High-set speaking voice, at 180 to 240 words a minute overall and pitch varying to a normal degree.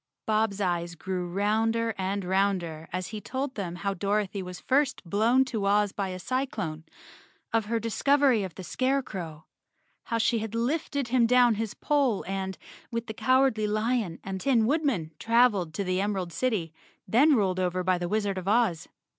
No: high, 210 Hz; average, 170 wpm; average, 4.2 semitones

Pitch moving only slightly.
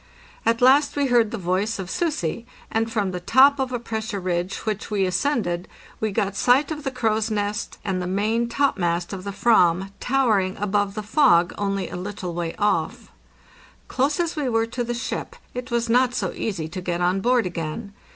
No: average, 4.7 semitones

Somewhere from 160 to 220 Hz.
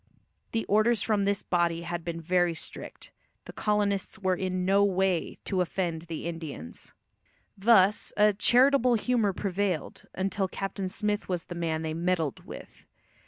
Yes: high, 190 Hz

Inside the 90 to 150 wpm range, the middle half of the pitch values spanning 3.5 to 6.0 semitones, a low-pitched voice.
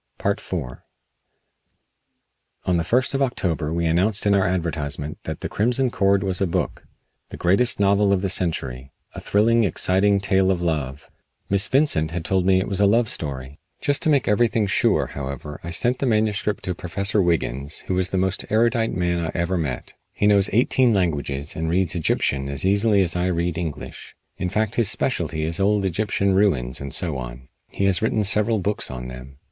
No: average, 190 wpm; average, 4.3 semitones; very low, 95 Hz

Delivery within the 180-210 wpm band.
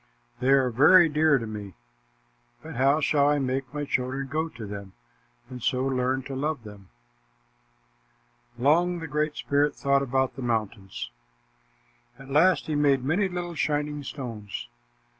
No: average, 150 wpm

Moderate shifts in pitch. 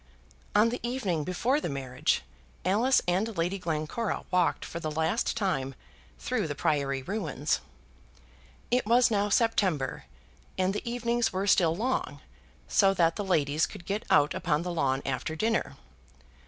No: wide, 6.3 semitones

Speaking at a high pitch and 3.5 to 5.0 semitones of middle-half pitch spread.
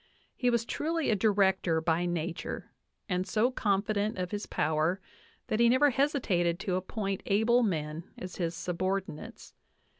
Yes: high, 195 Hz; average, 4.2 semitones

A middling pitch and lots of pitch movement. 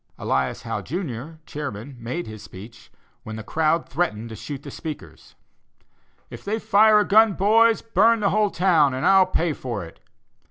Yes: medium, 160 Hz; wide, 9.0 semitones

